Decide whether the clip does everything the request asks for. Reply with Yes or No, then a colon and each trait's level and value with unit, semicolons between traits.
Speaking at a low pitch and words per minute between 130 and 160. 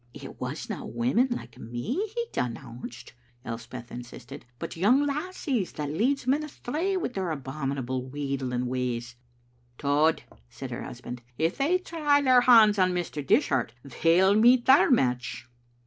No: medium, 155 Hz; average, 150 wpm